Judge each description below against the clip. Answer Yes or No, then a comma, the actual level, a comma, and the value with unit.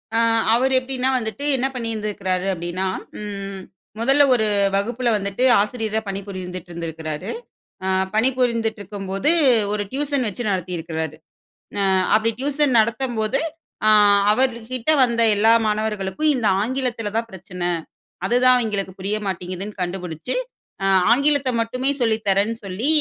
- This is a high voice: Yes, high, 220 Hz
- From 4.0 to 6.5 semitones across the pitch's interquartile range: Yes, average, 4.6 semitones